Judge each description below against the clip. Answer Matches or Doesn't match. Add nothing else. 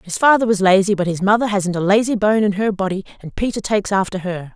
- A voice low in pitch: Doesn't match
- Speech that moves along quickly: Matches